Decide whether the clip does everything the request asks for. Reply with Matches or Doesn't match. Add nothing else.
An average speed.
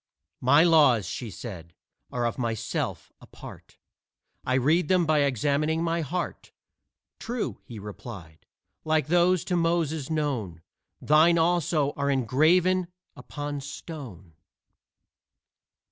Doesn't match